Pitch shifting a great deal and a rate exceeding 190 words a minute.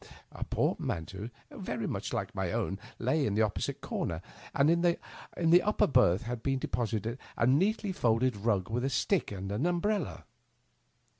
No: wide, 7.9 semitones; average, 150 wpm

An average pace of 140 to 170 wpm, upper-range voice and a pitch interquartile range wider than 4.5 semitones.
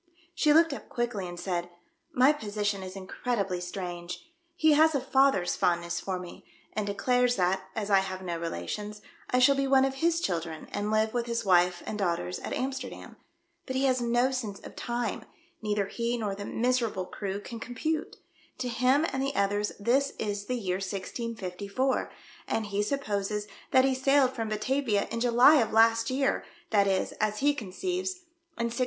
No: average, 185 wpm; high, 220 Hz; average, 4.9 semitones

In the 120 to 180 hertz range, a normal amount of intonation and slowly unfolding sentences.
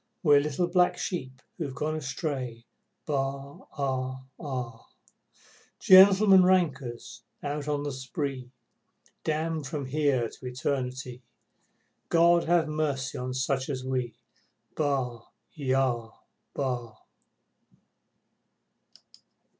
Yes: medium, 140 Hz; average, 3.1 semitones; slow, 95 wpm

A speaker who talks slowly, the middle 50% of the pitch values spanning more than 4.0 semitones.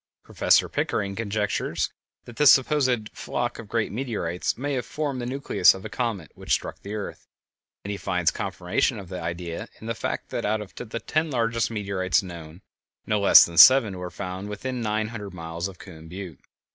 No: average, 190 wpm; average, 4.4 semitones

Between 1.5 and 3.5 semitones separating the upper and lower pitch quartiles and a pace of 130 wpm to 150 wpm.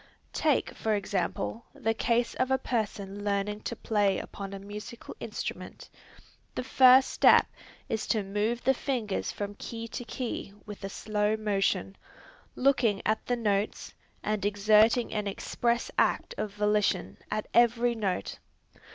Yes: narrow, 2.6 semitones; average, 145 wpm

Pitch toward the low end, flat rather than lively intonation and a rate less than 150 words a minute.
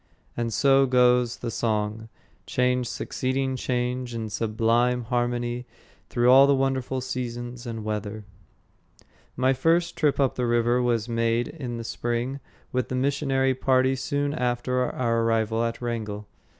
Yes: low, 125 Hz; narrow, 2.0 semitones; average, 140 wpm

